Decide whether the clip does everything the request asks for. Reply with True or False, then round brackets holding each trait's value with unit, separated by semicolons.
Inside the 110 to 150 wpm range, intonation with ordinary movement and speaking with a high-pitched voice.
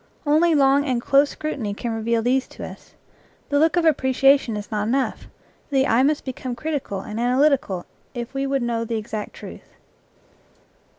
False (170 wpm; 3.7 semitones; 260 Hz)